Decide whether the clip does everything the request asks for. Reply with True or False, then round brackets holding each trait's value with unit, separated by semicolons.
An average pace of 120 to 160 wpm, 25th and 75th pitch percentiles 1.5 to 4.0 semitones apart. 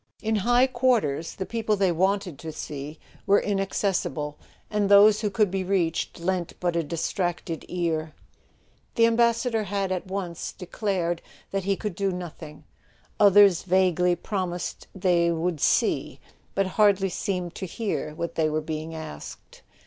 True (145 wpm; 3.3 semitones)